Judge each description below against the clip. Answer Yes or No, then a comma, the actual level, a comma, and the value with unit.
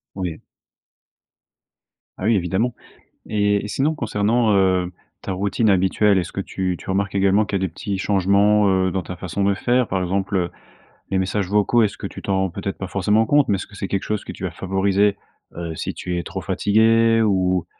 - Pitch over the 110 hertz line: No, low, 100 Hz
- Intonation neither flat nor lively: No, narrow, 2.0 semitones